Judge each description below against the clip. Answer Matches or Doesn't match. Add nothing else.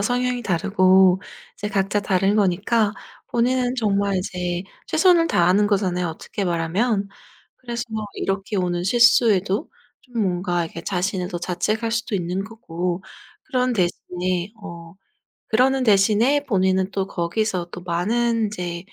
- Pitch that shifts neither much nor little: Matches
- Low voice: Doesn't match